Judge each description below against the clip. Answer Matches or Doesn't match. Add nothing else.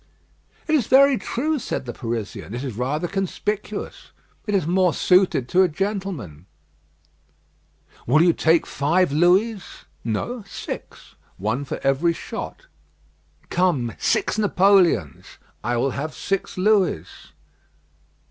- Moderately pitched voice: Matches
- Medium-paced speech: Doesn't match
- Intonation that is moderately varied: Doesn't match